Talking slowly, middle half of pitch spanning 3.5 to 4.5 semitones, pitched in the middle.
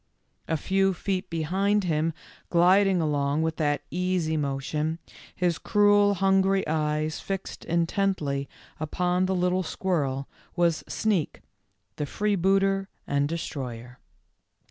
Yes: slow, 115 wpm; average, 4.1 semitones; medium, 170 Hz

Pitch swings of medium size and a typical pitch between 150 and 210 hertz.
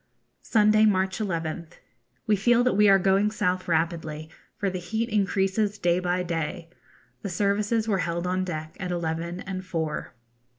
Yes: average, 3.3 semitones; medium, 185 Hz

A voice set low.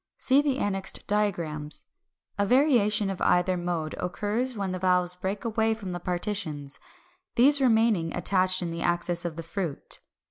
No: high, 190 Hz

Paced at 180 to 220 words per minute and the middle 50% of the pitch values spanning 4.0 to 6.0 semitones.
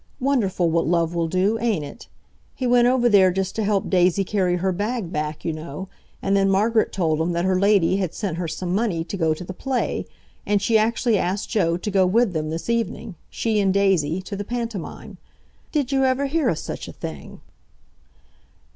Yes: average, 200 wpm; average, 4.6 semitones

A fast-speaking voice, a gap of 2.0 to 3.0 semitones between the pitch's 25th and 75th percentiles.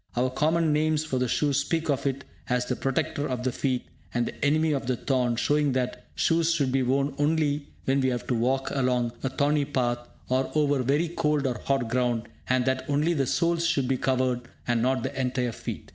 Yes: fast, 215 wpm; average, 2.7 semitones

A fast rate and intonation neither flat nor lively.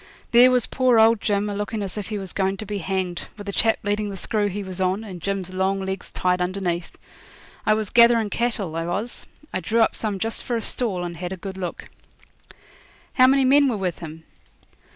Yes: fast, 220 wpm; average, 3.2 semitones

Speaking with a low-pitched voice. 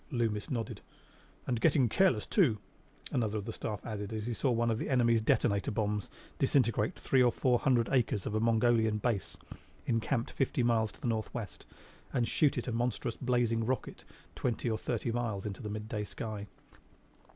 Yes: low, 115 Hz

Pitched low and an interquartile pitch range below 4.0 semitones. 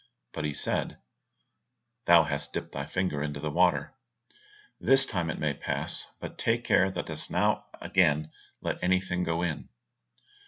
Yes: very low, 85 Hz; average, 3.6 semitones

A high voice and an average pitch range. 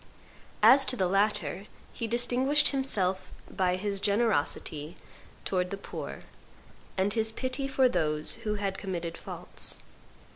Yes: high, 205 Hz; average, 4.6 semitones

